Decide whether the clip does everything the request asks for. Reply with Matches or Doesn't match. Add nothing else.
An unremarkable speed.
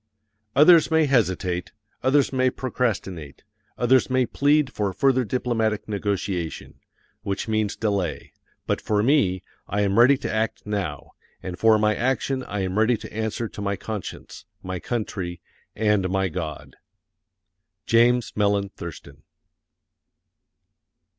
Doesn't match